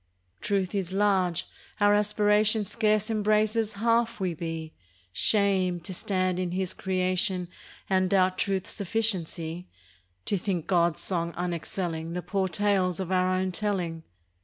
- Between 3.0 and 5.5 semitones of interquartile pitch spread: No, narrow, 2.6 semitones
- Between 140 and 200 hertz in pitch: Yes, high, 190 Hz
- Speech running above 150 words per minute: No, slow, 135 wpm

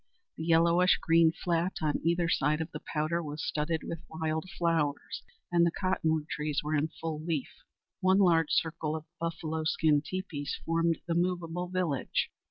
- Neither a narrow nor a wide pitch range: No, narrow, 1.7 semitones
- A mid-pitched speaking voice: Yes, medium, 165 Hz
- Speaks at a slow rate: No, average, 165 wpm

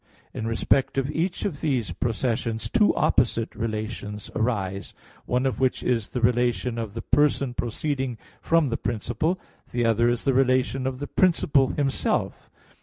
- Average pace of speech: Yes, average, 155 wpm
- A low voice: Yes, low, 125 Hz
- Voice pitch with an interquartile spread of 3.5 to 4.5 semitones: No, average, 3.0 semitones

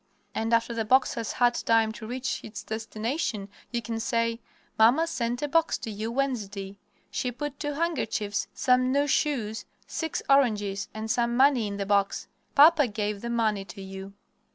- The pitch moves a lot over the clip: No, average, 3.7 semitones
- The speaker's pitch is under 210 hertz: No, high, 230 Hz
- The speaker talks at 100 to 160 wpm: No, average, 175 wpm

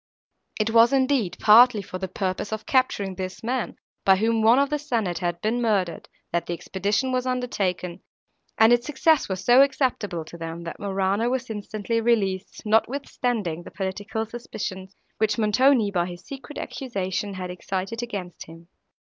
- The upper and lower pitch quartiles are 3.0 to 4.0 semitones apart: No, average, 4.4 semitones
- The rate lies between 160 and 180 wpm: Yes, average, 165 wpm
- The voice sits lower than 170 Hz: No, high, 210 Hz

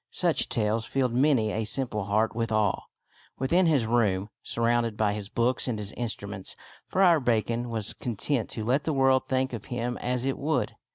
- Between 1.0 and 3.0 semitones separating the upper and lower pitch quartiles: No, average, 3.4 semitones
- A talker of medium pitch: No, low, 120 Hz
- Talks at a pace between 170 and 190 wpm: Yes, average, 180 wpm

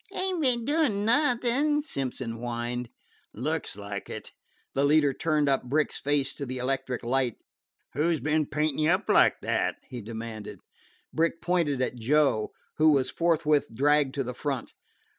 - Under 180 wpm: Yes, average, 160 wpm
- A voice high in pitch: No, medium, 145 Hz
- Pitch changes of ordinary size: Yes, average, 4.8 semitones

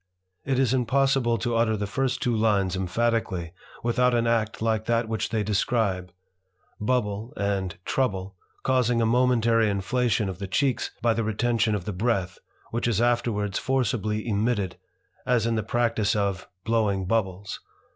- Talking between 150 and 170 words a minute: Yes, average, 155 wpm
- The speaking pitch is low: Yes, low, 115 Hz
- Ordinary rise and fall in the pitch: Yes, average, 3.0 semitones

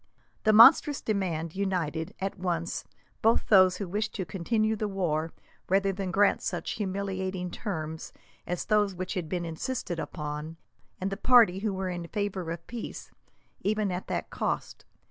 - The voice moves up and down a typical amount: Yes, average, 3.2 semitones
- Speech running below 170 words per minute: Yes, average, 160 wpm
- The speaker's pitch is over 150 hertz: Yes, high, 190 Hz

